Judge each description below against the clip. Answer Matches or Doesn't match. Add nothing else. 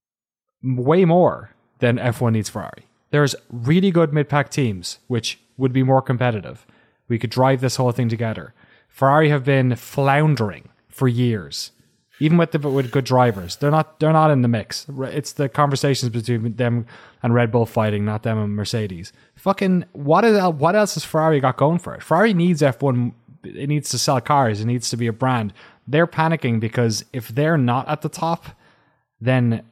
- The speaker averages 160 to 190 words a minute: Matches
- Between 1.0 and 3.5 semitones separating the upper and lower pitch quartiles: Doesn't match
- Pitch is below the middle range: Matches